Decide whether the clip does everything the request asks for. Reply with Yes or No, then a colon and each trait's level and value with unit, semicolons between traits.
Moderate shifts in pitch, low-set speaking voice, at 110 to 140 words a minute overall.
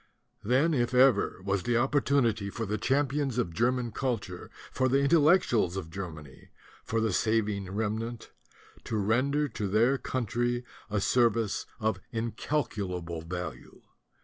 Yes: average, 4.4 semitones; low, 115 Hz; slow, 135 wpm